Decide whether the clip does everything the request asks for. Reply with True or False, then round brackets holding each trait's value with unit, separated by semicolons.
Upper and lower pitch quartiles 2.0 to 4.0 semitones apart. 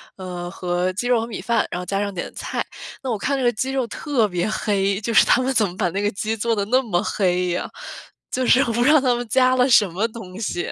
False (4.7 semitones)